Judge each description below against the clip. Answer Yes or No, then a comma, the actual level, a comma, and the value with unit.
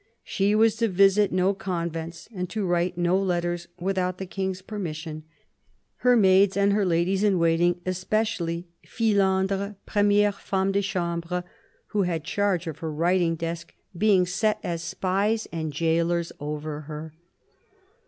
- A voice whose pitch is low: No, medium, 185 Hz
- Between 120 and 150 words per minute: Yes, average, 145 wpm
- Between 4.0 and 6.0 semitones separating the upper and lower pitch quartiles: No, average, 2.8 semitones